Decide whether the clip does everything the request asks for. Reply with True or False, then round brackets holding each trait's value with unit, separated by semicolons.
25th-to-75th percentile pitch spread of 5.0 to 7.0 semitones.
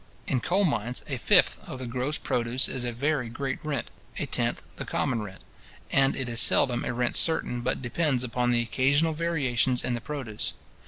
False (2.9 semitones)